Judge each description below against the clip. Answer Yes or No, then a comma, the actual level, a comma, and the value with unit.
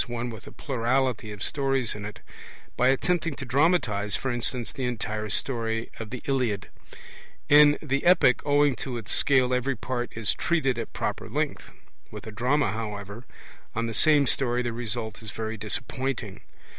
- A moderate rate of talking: Yes, average, 170 wpm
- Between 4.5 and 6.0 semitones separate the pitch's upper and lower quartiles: No, average, 3.4 semitones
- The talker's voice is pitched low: Yes, low, 120 Hz